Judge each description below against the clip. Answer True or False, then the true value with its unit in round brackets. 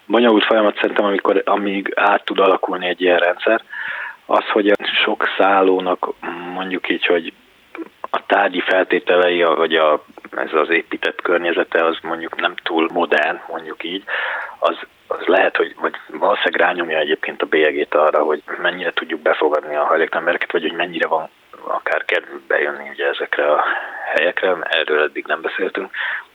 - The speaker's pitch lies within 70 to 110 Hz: True (90 Hz)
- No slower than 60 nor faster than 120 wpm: False (150 wpm)